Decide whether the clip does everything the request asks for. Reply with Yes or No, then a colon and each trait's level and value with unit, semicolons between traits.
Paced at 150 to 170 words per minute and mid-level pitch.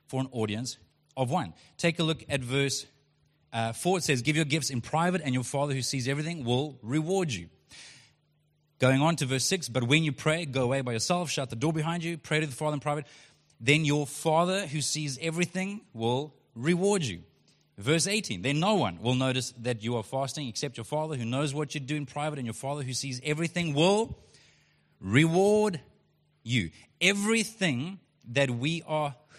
No: average, 195 wpm; medium, 145 Hz